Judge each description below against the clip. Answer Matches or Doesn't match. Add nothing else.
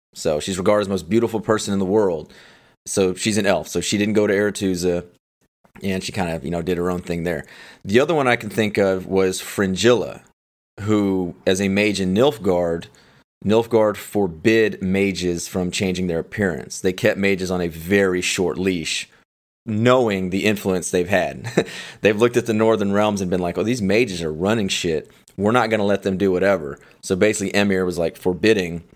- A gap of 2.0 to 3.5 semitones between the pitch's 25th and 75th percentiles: Matches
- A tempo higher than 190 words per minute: Matches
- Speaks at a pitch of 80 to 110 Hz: Matches